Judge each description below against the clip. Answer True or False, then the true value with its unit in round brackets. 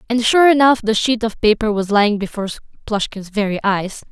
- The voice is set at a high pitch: True (220 Hz)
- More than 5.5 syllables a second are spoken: True (5.8 syllables/s)